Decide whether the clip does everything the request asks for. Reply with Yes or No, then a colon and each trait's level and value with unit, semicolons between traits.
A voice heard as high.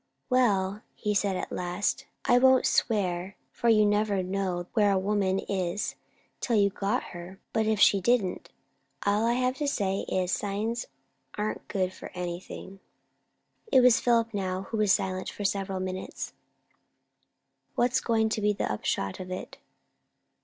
Yes: high, 200 Hz